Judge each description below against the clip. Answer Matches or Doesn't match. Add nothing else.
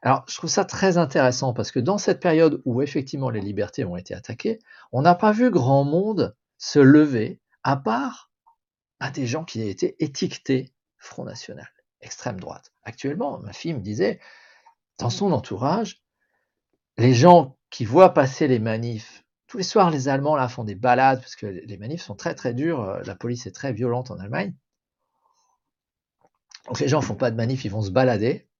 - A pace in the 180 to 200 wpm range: Matches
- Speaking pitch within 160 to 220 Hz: Doesn't match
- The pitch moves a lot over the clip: Matches